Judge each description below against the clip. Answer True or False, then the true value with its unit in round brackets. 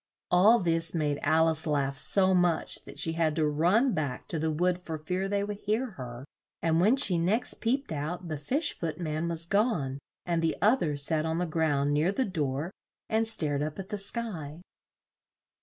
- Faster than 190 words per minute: True (200 wpm)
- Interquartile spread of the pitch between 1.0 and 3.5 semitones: False (4.4 semitones)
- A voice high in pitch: False (165 Hz)